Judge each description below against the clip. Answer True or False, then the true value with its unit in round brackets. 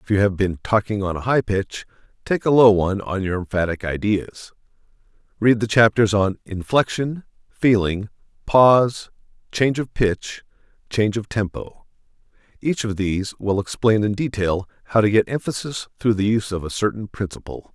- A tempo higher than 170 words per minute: False (160 wpm)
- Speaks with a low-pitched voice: True (105 Hz)